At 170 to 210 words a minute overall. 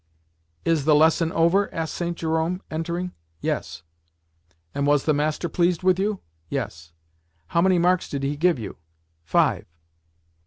No: average, 145 wpm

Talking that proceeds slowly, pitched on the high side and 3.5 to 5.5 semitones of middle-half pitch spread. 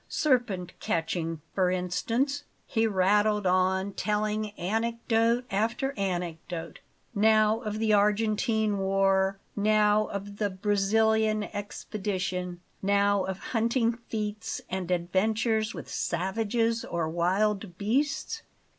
No: slow, 105 wpm; high, 210 Hz; average, 2.8 semitones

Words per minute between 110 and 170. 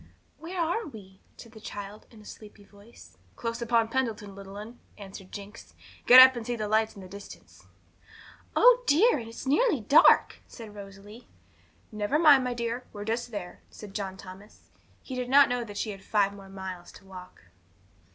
No: average, 185 wpm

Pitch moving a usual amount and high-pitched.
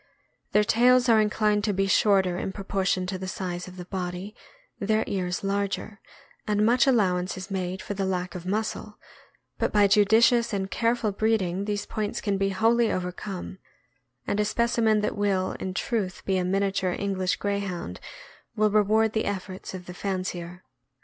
No: narrow, 2.3 semitones; high, 200 Hz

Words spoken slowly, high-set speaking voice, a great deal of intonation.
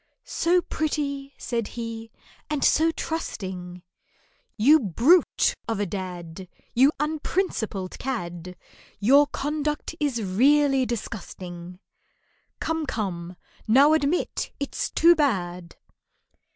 Yes: slow, 100 wpm; high, 240 Hz; wide, 8.0 semitones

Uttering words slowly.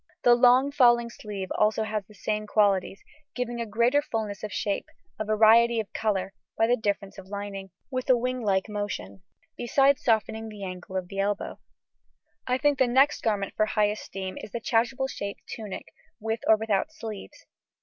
No: average, 175 wpm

